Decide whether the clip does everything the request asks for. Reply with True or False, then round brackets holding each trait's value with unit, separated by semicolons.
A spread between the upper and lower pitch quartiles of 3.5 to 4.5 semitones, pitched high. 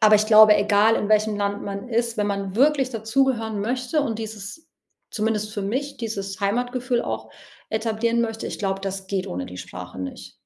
False (2.8 semitones; 215 Hz)